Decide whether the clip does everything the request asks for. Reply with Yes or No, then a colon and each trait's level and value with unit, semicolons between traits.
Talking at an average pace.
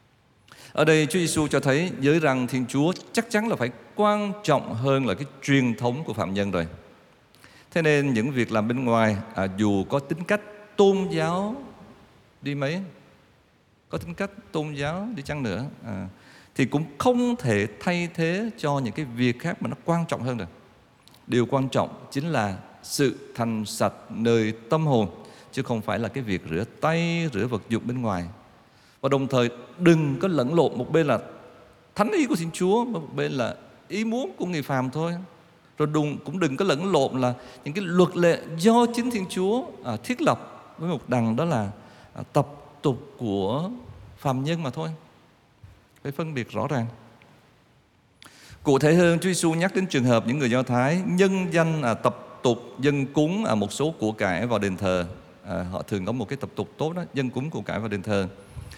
Yes: average, 200 wpm